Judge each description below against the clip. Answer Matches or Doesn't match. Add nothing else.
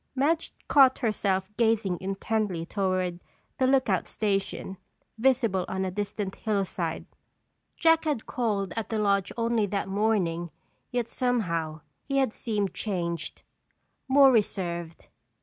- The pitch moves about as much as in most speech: Matches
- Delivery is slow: Matches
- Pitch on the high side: Matches